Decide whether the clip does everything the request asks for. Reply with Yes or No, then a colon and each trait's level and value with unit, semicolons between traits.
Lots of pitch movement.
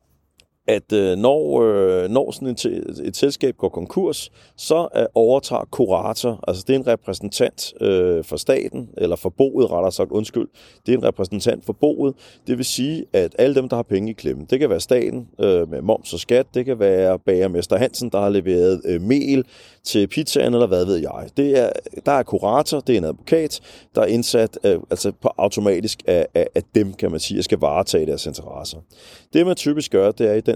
Yes: wide, 7.1 semitones